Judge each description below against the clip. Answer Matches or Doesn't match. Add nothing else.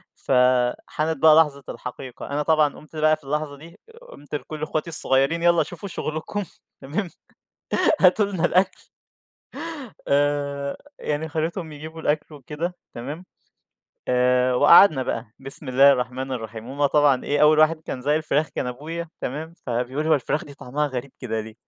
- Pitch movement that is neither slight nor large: Matches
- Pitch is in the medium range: Matches